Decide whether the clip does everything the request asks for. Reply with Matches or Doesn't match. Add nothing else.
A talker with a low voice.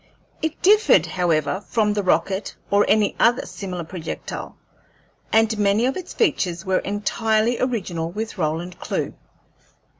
Doesn't match